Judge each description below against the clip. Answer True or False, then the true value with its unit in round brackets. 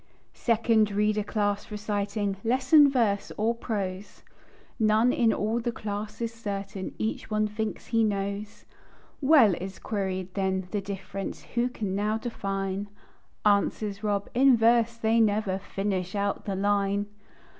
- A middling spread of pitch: False (2.2 semitones)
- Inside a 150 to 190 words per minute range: False (135 wpm)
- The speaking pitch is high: True (210 Hz)